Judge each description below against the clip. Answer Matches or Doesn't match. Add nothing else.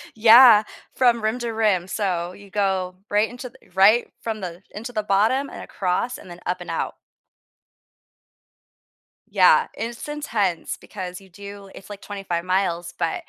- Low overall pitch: Doesn't match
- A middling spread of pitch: Matches